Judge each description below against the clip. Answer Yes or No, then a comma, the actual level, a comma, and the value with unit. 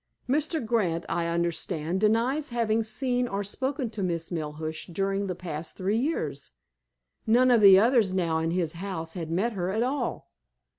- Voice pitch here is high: Yes, high, 195 Hz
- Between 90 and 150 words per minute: No, average, 165 wpm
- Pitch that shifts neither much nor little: No, wide, 5.8 semitones